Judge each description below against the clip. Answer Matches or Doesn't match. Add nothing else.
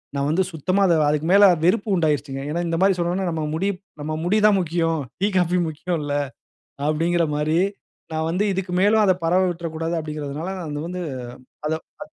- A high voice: Doesn't match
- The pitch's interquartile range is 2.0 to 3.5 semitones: Matches